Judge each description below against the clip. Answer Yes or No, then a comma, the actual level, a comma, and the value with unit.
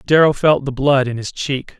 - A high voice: No, low, 135 Hz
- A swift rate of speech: Yes, fast, 235 wpm